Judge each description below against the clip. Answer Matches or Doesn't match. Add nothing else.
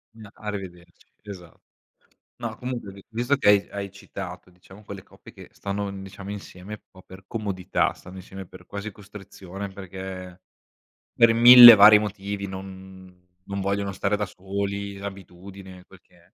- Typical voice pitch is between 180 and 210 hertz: Doesn't match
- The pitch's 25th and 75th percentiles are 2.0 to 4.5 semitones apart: Doesn't match